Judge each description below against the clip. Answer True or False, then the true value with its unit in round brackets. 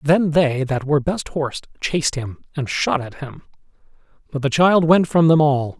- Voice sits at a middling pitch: True (145 Hz)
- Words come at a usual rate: True (195 wpm)